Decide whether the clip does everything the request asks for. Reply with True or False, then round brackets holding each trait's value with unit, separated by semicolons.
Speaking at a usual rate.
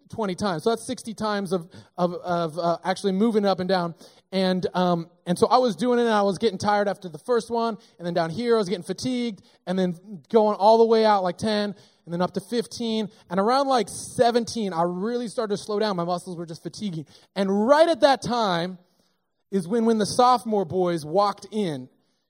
False (220 wpm)